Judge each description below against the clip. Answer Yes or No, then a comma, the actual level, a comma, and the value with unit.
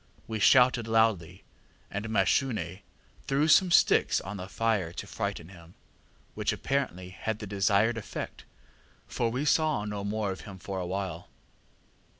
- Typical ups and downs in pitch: Yes, average, 3.3 semitones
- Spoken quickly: No, average, 150 wpm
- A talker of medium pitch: No, low, 105 Hz